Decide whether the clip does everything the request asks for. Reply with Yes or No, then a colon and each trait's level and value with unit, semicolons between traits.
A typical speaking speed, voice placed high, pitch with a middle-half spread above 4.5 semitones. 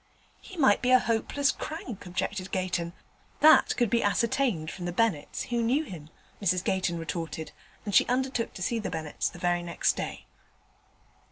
Yes: average, 170 wpm; high, 195 Hz; wide, 5.5 semitones